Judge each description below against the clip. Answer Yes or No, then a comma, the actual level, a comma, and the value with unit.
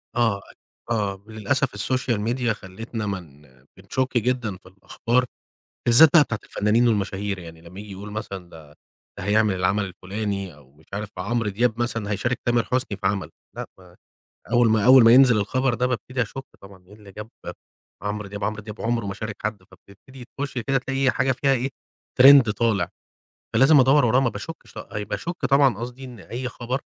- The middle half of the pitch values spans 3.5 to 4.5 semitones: Yes, average, 4.1 semitones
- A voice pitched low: Yes, low, 110 Hz